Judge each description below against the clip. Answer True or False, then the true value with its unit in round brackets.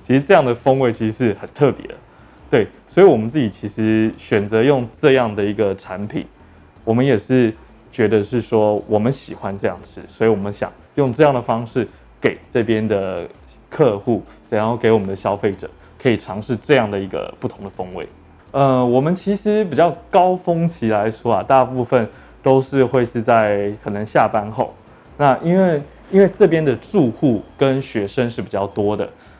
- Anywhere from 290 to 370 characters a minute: False (270 characters per minute)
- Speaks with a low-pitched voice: True (120 Hz)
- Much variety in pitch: False (4.1 semitones)